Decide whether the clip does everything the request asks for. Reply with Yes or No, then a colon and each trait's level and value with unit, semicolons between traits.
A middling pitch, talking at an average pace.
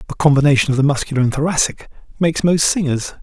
Yes: medium, 145 Hz; average, 185 wpm